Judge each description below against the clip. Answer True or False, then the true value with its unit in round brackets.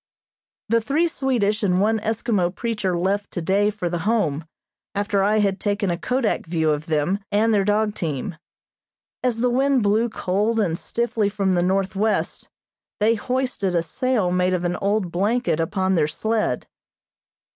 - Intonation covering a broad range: False (3.6 semitones)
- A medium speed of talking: True (160 wpm)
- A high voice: True (205 Hz)